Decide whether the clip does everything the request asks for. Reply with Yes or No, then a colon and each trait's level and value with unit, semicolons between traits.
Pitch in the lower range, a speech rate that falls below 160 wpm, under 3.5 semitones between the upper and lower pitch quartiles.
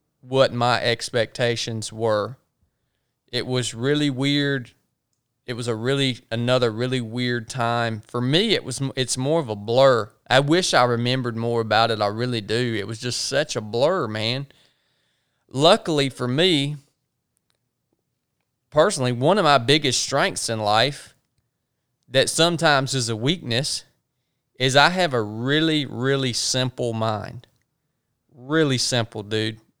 Yes: low, 125 Hz; average, 140 wpm; average, 2.9 semitones